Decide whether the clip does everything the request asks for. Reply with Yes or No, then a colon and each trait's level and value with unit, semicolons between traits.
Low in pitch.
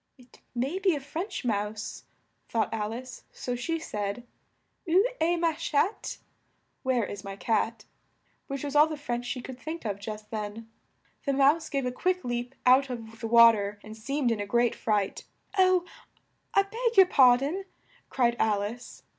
No: high, 245 Hz